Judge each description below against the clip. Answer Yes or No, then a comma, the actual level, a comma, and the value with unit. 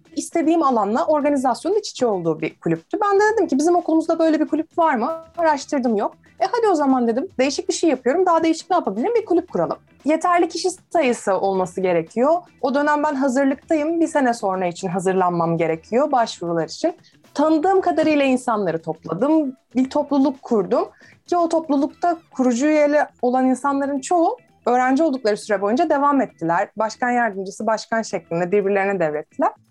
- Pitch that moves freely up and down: Yes, wide, 7.4 semitones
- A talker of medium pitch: No, very high, 275 Hz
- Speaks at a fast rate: Yes, fast, 165 wpm